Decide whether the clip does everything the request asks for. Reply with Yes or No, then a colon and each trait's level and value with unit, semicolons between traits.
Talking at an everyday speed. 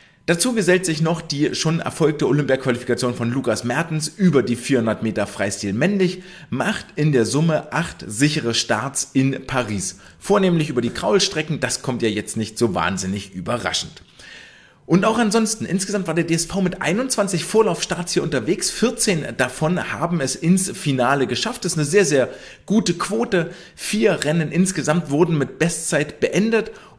Yes: average, 160 wpm